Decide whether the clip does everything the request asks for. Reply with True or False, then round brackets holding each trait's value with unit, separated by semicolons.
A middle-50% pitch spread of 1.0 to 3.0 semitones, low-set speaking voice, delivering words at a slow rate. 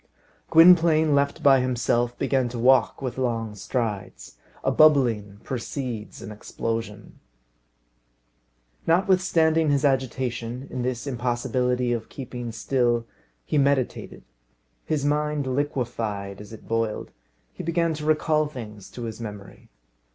False (4.0 semitones; 125 Hz; 120 wpm)